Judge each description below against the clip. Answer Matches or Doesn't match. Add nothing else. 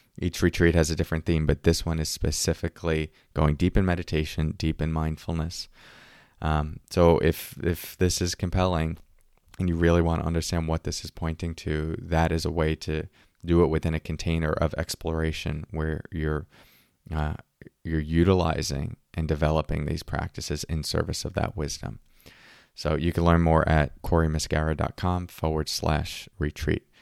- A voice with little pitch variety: Matches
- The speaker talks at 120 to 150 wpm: Doesn't match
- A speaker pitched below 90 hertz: Matches